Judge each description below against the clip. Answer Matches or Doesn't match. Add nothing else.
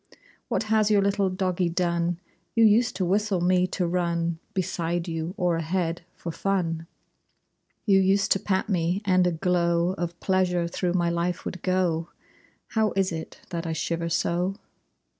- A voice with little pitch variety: Matches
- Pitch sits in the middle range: Matches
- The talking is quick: Doesn't match